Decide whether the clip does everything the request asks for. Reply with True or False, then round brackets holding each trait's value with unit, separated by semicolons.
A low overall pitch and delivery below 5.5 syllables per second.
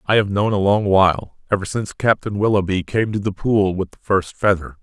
False (100 Hz; 5.6 syllables/s)